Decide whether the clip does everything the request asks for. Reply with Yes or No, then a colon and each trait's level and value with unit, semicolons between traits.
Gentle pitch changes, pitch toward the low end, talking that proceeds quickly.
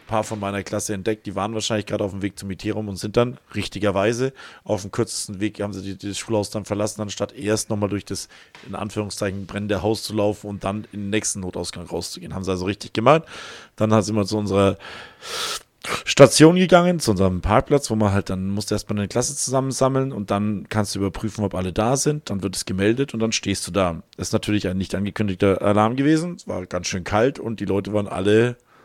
Yes: narrow, 1.8 semitones; low, 105 Hz; fast, 230 wpm